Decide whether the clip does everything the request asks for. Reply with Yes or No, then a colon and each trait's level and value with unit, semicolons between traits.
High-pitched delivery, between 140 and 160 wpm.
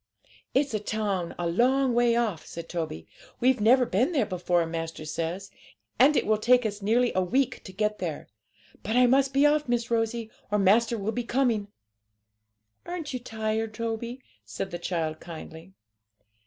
No: high, 220 Hz; average, 170 wpm